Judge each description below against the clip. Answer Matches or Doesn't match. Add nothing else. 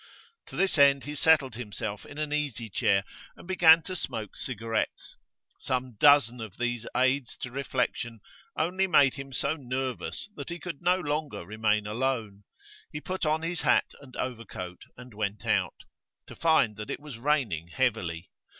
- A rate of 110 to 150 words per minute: Doesn't match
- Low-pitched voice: Matches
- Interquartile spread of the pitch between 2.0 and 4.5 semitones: Doesn't match